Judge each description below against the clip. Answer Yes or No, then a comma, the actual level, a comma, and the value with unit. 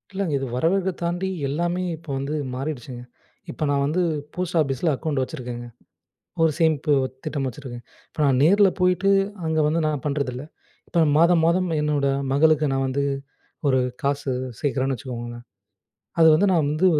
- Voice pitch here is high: No, medium, 150 Hz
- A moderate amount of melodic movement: Yes, average, 3.9 semitones